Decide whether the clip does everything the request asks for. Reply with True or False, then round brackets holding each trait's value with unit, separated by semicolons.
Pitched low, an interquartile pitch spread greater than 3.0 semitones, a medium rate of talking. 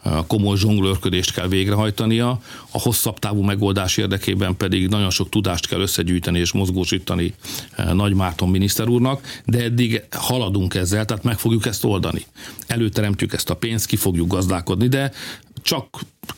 True (100 Hz; 3.6 semitones; 145 wpm)